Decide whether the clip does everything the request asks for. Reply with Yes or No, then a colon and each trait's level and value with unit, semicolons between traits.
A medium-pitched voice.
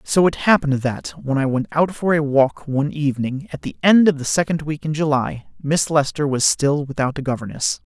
Yes: medium, 145 Hz